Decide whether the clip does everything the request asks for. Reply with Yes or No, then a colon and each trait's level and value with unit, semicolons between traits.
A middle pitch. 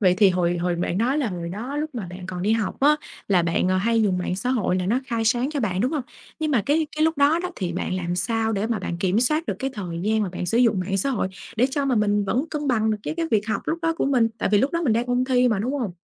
No: high, 225 Hz